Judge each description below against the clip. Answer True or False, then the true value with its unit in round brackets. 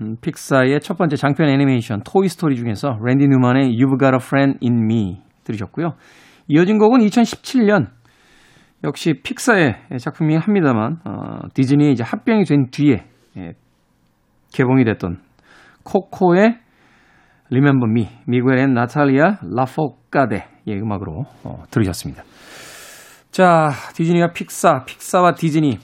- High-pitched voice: False (140 Hz)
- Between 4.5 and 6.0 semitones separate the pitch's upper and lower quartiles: True (5.5 semitones)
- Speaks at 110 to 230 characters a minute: False (315 characters per minute)